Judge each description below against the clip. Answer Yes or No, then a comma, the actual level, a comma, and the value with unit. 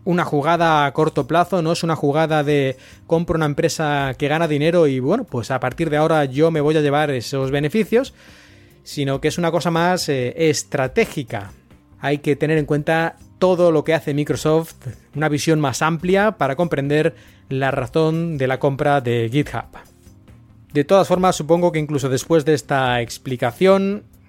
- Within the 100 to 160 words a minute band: No, average, 175 wpm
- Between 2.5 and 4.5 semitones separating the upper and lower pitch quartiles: Yes, average, 3.6 semitones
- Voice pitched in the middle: Yes, medium, 150 Hz